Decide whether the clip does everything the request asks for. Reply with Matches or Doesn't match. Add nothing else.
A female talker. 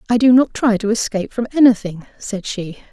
Matches